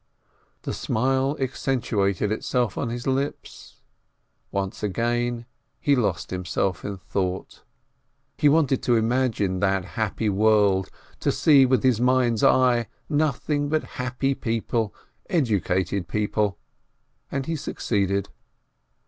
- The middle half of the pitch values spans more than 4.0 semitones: Yes, average, 4.8 semitones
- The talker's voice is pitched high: No, low, 115 Hz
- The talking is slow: Yes, slow, 115 wpm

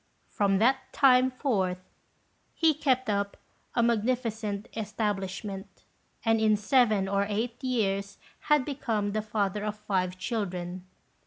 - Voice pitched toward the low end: No, high, 210 Hz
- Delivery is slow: Yes, slow, 120 wpm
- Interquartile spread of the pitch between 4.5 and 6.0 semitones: No, average, 3.5 semitones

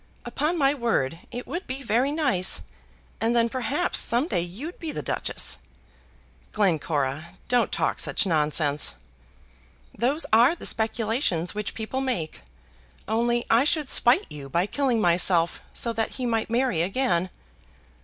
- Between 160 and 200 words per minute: No, average, 145 wpm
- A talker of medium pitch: No, high, 230 Hz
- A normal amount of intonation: No, wide, 7.0 semitones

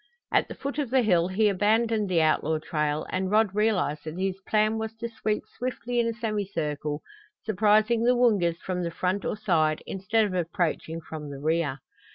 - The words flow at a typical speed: Yes, average, 190 wpm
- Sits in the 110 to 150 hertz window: No, high, 195 Hz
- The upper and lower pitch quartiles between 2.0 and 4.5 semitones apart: No, average, 5.1 semitones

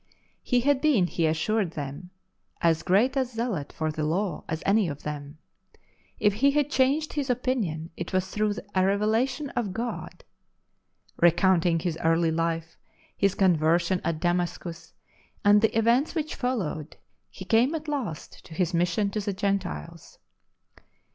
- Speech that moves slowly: No, average, 150 wpm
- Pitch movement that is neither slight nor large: No, wide, 6.3 semitones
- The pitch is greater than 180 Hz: Yes, high, 190 Hz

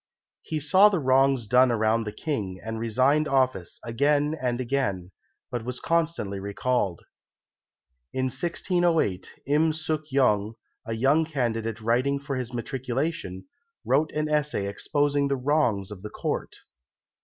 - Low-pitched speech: Yes, low, 130 Hz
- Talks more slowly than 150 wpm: Yes, slow, 135 wpm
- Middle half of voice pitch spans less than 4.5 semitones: No, average, 5.0 semitones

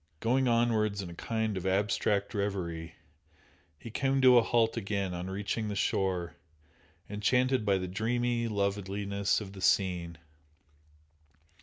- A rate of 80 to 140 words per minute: Yes, slow, 135 wpm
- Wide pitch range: No, average, 3.3 semitones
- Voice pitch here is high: No, low, 100 Hz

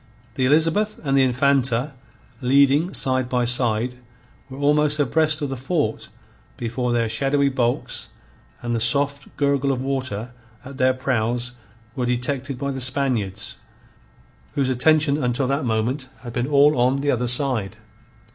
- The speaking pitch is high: No, low, 130 Hz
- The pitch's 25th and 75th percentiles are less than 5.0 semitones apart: Yes, narrow, 2.4 semitones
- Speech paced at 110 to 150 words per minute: Yes, average, 145 wpm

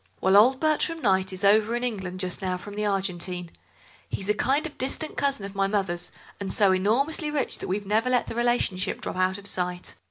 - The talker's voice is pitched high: Yes, high, 200 Hz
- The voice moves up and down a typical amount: Yes, average, 4.6 semitones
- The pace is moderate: No, fast, 215 wpm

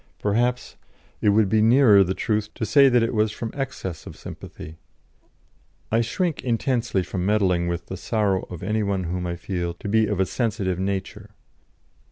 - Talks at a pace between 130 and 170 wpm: No, average, 180 wpm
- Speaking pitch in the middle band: No, low, 105 Hz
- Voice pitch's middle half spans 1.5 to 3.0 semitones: No, average, 3.5 semitones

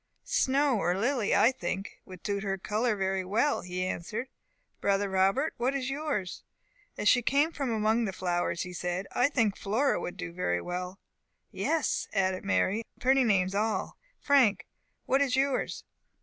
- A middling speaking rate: Yes, average, 170 wpm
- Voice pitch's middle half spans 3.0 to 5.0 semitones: No, wide, 5.6 semitones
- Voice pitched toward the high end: Yes, high, 210 Hz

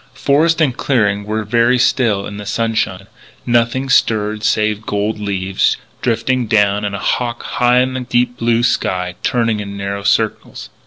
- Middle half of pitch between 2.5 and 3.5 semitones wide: Yes, average, 3.1 semitones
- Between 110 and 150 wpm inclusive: No, average, 160 wpm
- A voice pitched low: Yes, low, 110 Hz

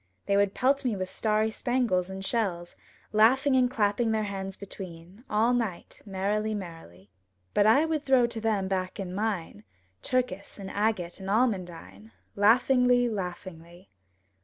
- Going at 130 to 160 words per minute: Yes, average, 145 wpm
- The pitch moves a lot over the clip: No, average, 4.1 semitones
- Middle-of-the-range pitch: No, high, 205 Hz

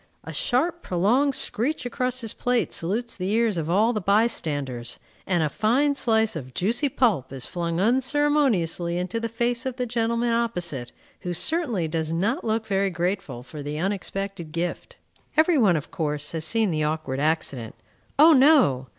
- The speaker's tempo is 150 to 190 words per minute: Yes, average, 170 wpm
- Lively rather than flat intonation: Yes, wide, 6.7 semitones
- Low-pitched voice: No, high, 200 Hz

